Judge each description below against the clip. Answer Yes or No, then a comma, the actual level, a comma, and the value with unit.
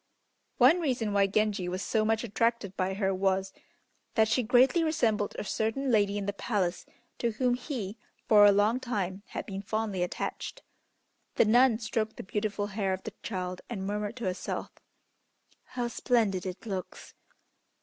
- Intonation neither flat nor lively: Yes, average, 3.2 semitones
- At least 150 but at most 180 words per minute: Yes, average, 165 wpm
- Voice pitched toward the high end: Yes, high, 210 Hz